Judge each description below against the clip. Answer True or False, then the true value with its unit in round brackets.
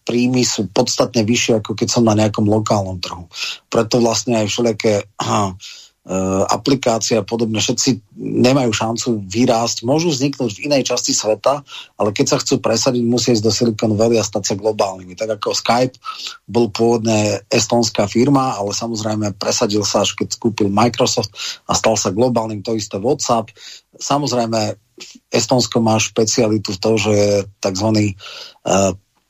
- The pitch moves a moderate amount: False (2.3 semitones)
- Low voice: True (115 Hz)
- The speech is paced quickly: False (155 wpm)